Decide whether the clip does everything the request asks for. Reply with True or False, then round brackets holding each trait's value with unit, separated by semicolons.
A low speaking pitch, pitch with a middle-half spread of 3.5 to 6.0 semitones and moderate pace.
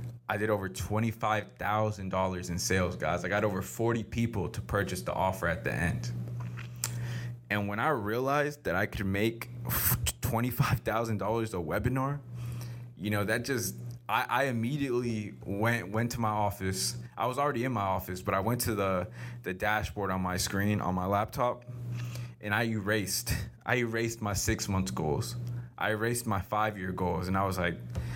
True (110 Hz; 4.0 semitones; 170 wpm)